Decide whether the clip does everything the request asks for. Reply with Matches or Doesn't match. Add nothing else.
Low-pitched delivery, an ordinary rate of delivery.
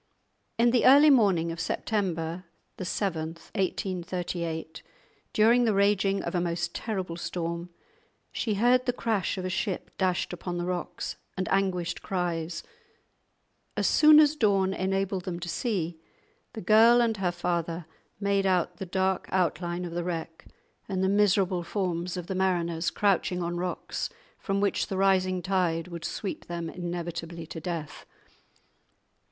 Doesn't match